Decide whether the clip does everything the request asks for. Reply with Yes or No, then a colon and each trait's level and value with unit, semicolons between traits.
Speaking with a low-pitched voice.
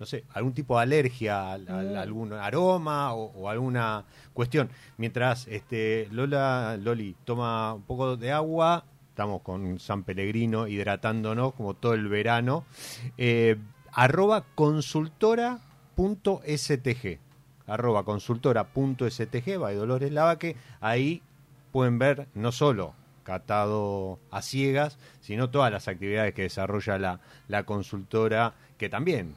Yes: low, 120 Hz